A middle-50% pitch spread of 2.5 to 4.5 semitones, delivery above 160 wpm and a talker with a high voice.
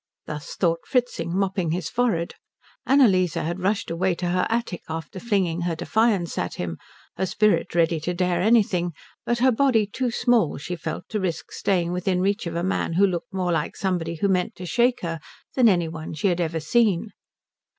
No: average, 3.9 semitones; average, 190 wpm; medium, 180 Hz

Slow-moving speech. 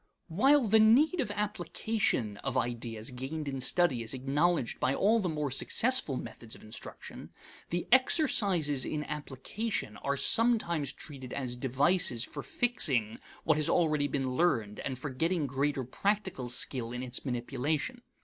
No: average, 150 wpm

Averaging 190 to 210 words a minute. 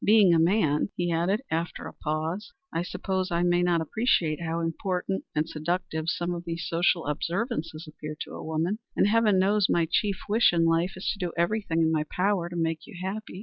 Yes: fast, 205 wpm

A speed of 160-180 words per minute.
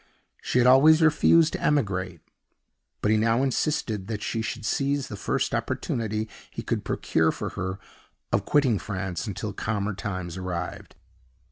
No: average, 150 wpm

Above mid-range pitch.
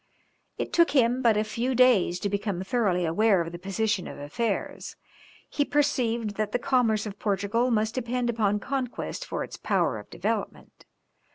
Yes: high, 220 Hz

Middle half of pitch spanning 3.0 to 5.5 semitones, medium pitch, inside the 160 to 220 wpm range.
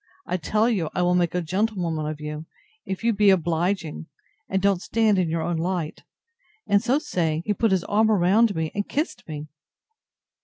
Yes: average, 4.3 semitones; medium, 180 Hz; average, 190 wpm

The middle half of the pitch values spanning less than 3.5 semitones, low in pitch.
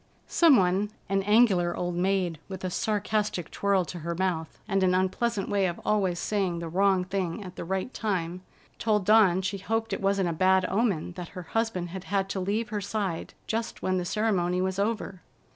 No: narrow, 2.5 semitones; high, 190 Hz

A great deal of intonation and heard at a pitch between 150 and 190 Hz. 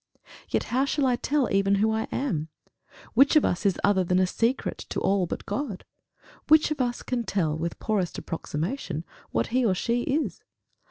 No: wide, 6.0 semitones; high, 220 Hz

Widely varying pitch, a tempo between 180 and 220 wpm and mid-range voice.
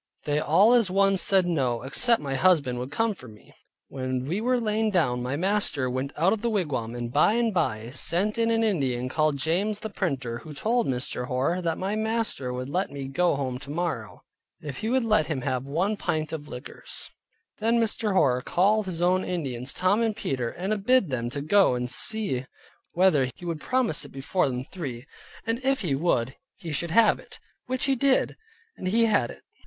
Yes: wide, 8.3 semitones; average, 200 wpm; medium, 170 Hz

